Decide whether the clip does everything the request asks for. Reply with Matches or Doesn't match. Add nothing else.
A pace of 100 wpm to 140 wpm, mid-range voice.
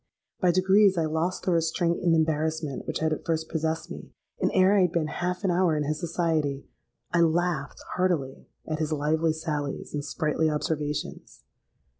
Doesn't match